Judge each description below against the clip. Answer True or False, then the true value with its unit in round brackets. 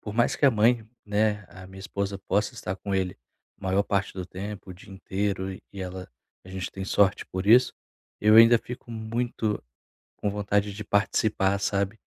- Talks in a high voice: False (100 Hz)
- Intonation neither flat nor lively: False (2.1 semitones)